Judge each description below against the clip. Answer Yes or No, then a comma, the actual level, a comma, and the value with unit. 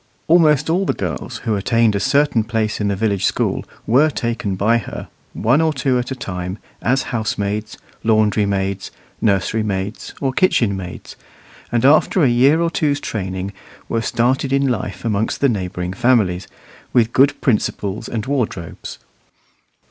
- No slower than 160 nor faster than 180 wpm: No, average, 150 wpm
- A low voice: Yes, low, 115 Hz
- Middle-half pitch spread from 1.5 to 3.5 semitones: No, average, 4.9 semitones